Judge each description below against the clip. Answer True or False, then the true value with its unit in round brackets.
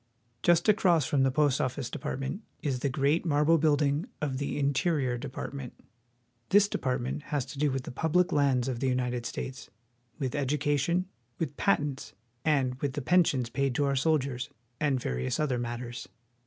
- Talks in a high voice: False (140 Hz)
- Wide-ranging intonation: False (2.9 semitones)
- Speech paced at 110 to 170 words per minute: True (165 wpm)